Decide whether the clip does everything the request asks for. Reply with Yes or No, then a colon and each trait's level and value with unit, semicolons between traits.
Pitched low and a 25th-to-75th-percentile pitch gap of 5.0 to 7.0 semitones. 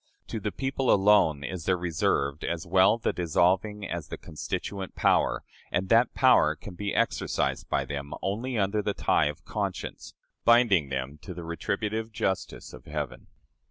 Yes: very low, 95 Hz; wide, 5.4 semitones